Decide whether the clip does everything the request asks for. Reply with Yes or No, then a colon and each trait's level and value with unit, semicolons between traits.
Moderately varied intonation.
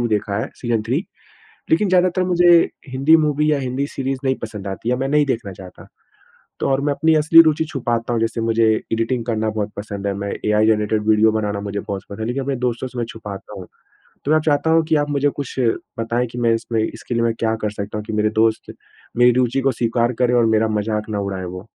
Yes: average, 4.2 semitones